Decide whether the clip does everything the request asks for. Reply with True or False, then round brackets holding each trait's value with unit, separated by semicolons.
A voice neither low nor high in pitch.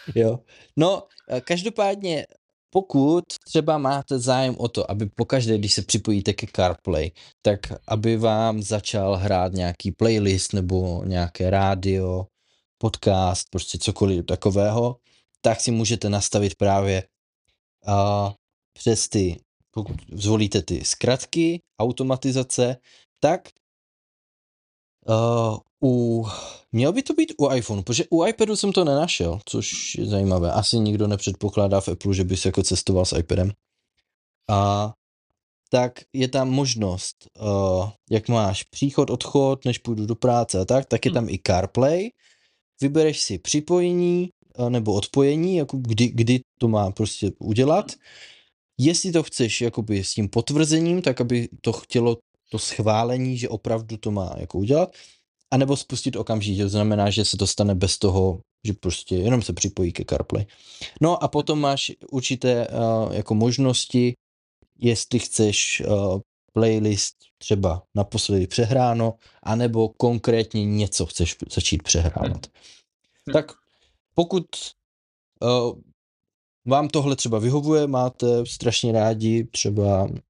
False (115 Hz)